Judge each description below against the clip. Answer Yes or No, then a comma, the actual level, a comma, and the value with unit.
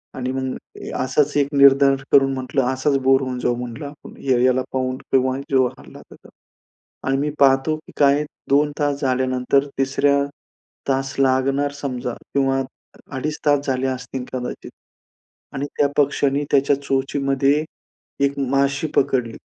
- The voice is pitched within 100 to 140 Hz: Yes, low, 135 Hz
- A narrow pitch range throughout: Yes, narrow, 1.4 semitones